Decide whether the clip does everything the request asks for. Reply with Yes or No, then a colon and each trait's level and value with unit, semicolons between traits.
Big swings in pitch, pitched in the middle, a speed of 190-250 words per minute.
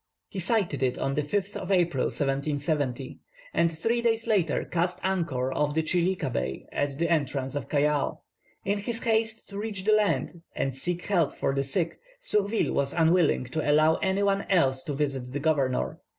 No: wide, 5.9 semitones; medium, 160 Hz; average, 180 wpm